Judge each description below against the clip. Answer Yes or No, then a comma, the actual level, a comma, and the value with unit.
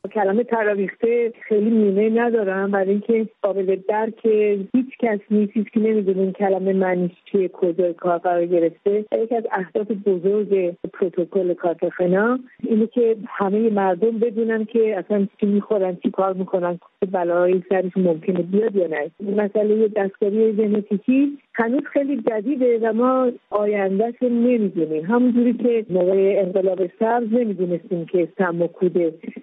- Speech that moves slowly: No, average, 140 wpm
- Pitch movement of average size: Yes, average, 3.2 semitones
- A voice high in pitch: Yes, high, 205 Hz